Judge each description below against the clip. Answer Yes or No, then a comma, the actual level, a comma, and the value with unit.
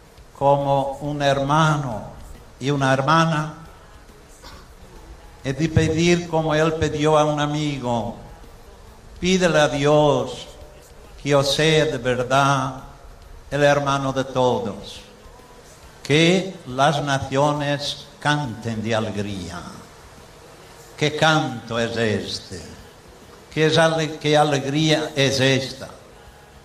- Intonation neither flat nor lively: No, wide, 6.5 semitones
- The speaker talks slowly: Yes, slow, 100 wpm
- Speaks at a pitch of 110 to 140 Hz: Yes, low, 135 Hz